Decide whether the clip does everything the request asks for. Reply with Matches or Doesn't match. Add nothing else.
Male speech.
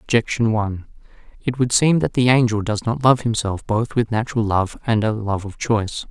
Matches